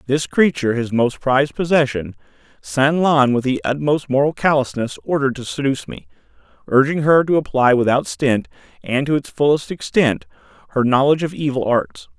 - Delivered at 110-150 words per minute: No, average, 160 wpm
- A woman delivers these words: No, male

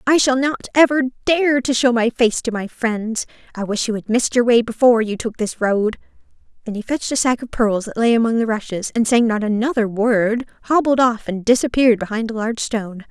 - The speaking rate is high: Yes, fast, 225 wpm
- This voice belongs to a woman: Yes, female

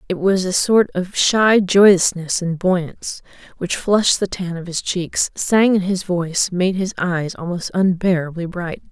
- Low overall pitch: No, medium, 180 Hz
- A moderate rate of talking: Yes, average, 175 wpm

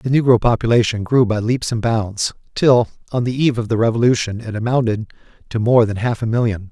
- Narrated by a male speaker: Yes, male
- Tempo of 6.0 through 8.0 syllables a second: Yes, 6.1 syllables/s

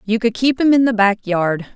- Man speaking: No, female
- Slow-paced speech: No, fast, 275 wpm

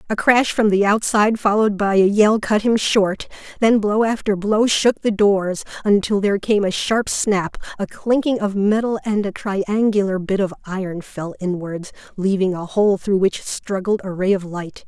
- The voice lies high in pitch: Yes, high, 200 Hz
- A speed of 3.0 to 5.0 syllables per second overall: Yes, 4.6 syllables/s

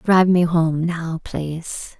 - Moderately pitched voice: Yes, medium, 165 Hz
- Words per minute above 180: No, average, 150 wpm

